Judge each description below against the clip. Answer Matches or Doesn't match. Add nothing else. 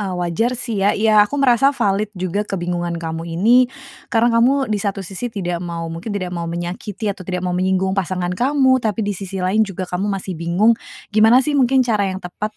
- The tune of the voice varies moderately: Matches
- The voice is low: Doesn't match